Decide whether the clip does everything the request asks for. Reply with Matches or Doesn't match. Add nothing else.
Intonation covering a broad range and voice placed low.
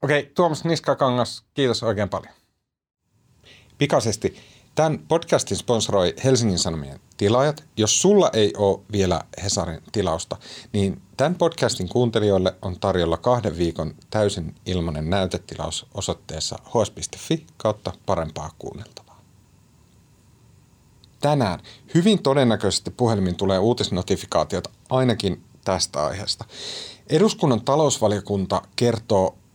Matches